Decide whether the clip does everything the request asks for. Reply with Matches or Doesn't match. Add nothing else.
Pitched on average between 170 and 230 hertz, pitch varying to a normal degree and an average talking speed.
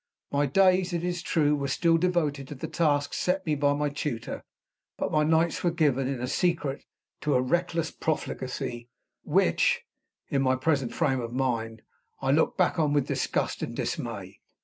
Doesn't match